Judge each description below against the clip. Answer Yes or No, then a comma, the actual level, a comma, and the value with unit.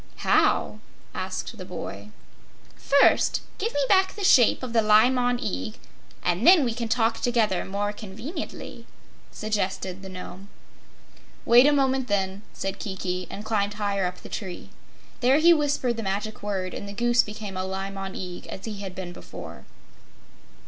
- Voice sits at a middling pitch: No, high, 210 Hz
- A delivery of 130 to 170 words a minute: Yes, average, 165 wpm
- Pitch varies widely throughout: No, average, 4.2 semitones